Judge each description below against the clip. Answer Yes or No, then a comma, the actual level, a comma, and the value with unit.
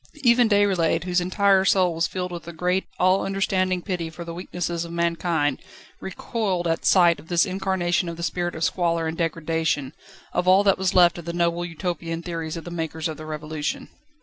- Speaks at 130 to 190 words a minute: No, average, 200 wpm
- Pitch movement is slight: Yes, narrow, 2.0 semitones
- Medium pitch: Yes, medium, 175 Hz